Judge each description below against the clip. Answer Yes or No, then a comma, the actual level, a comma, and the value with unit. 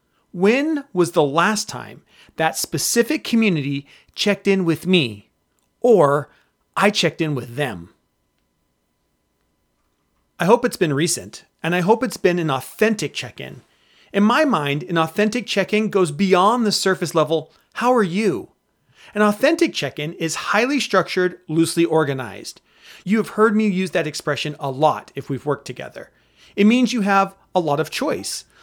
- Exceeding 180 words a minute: No, average, 160 wpm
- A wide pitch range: Yes, wide, 5.7 semitones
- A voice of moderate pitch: Yes, medium, 180 Hz